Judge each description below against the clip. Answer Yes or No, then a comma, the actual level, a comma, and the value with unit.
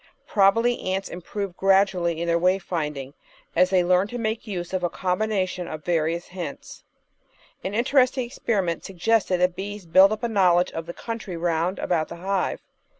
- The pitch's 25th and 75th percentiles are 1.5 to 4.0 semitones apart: Yes, average, 3.0 semitones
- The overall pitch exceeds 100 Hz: Yes, medium, 185 Hz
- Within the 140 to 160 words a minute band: No, average, 175 wpm